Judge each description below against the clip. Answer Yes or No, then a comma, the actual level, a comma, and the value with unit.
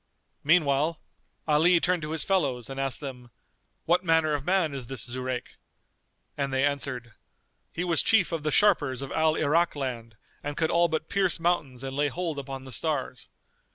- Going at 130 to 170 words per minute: No, average, 180 wpm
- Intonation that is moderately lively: Yes, average, 3.9 semitones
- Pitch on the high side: No, medium, 145 Hz